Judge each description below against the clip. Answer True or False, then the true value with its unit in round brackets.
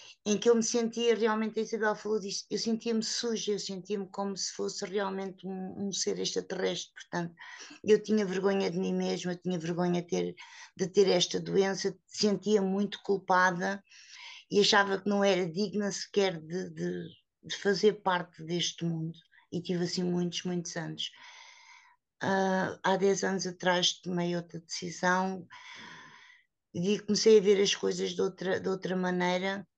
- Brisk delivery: False (165 wpm)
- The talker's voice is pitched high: True (195 Hz)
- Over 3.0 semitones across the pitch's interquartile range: False (2.6 semitones)